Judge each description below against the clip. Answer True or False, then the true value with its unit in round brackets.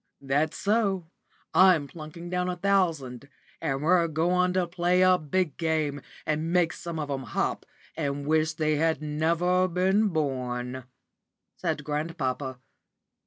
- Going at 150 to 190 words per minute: False (135 wpm)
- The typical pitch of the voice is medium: True (160 Hz)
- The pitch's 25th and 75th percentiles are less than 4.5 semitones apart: True (3.7 semitones)